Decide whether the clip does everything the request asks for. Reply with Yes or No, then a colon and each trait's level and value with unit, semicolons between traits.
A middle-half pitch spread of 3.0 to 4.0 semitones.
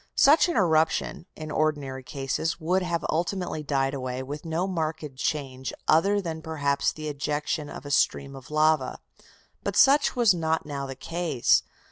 Yes: average, 3.3 semitones